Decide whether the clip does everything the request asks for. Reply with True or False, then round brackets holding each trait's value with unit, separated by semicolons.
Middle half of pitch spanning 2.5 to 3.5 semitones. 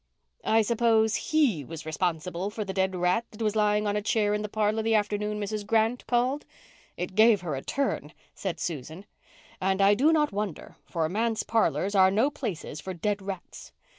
True (2.9 semitones)